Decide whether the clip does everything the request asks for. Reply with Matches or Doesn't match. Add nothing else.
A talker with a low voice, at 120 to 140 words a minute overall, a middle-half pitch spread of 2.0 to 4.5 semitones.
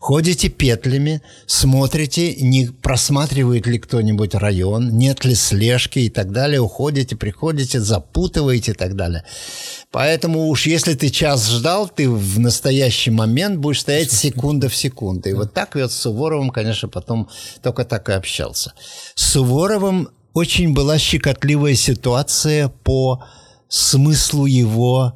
Matches